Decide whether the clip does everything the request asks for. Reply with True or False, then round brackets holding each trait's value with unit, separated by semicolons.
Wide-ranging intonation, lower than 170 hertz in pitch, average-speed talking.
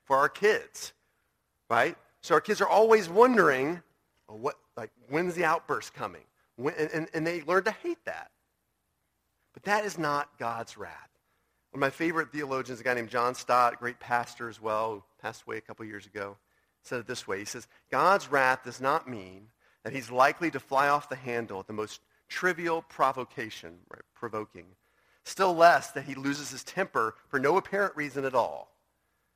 True (6.1 semitones; 135 Hz; 185 wpm)